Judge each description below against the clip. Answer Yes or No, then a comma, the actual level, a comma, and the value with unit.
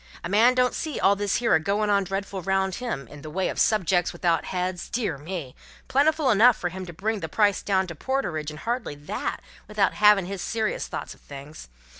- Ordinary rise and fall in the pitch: Yes, average, 4.0 semitones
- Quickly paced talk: Yes, fast, 210 wpm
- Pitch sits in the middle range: No, high, 195 Hz